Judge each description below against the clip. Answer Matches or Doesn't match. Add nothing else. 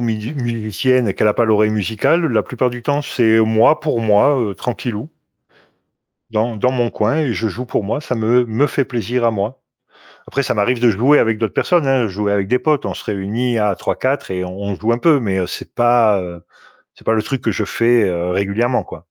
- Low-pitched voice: Matches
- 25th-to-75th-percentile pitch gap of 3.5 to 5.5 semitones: Doesn't match